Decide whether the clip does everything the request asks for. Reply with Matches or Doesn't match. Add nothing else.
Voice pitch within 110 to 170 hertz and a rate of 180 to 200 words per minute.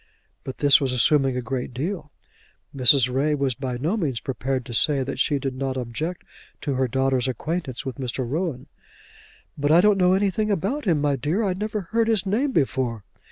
Matches